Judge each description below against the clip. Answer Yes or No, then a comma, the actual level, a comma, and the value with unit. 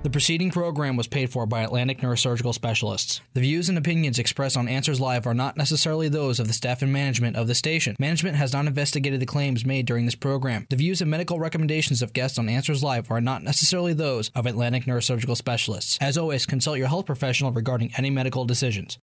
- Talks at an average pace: No, fast, 215 wpm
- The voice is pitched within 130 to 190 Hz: Yes, low, 135 Hz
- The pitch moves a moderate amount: Yes, average, 3.3 semitones